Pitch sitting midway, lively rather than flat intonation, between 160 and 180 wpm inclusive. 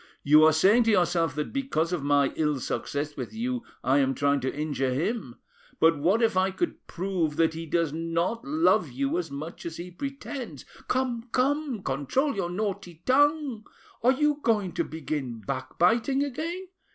Yes: medium, 175 Hz; wide, 8.2 semitones; average, 175 wpm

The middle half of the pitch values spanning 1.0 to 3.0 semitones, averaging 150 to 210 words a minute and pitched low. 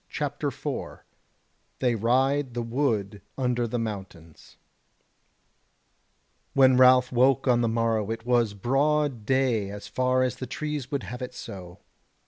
No: average, 2.7 semitones; slow, 135 wpm; low, 125 Hz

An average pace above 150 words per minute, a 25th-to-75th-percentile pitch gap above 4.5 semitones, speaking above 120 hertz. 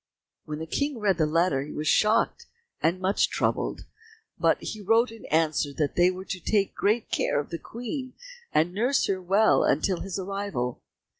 Yes: average, 180 wpm; average, 5.1 semitones; high, 190 Hz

